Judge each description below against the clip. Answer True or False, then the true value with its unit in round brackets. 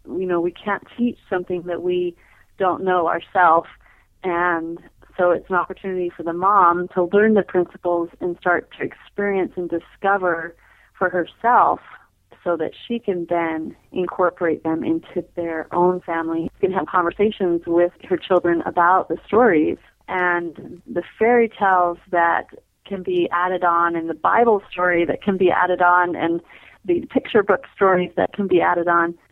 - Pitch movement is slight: True (1.7 semitones)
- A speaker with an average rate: True (165 wpm)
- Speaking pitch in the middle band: True (180 Hz)